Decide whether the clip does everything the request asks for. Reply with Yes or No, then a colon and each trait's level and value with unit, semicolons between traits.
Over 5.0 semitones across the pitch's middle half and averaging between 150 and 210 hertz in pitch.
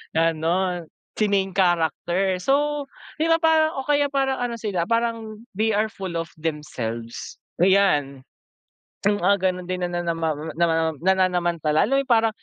Yes: wide, 5.4 semitones; medium, 185 Hz